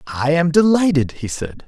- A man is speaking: Yes, male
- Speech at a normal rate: Yes, average, 180 wpm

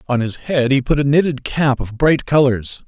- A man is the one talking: Yes, male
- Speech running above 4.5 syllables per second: Yes, 4.8 syllables/s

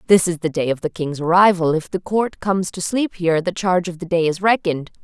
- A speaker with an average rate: No, fast, 260 wpm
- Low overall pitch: No, medium, 175 Hz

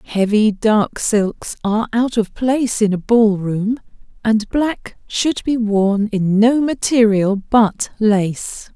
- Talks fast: No, average, 145 wpm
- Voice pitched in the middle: No, high, 220 Hz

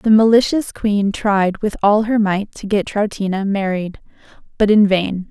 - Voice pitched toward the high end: Yes, high, 205 Hz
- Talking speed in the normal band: Yes, average, 170 wpm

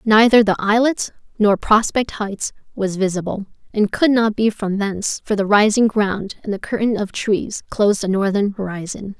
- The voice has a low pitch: No, high, 210 Hz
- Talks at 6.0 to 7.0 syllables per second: No, 4.8 syllables/s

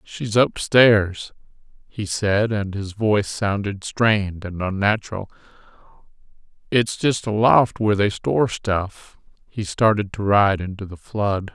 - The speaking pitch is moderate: No, low, 105 Hz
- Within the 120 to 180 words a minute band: Yes, slow, 135 wpm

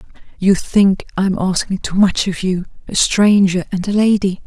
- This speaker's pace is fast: No, average, 190 wpm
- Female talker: Yes, female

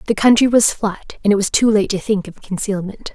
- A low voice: No, high, 205 Hz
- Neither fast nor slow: No, fast, 250 wpm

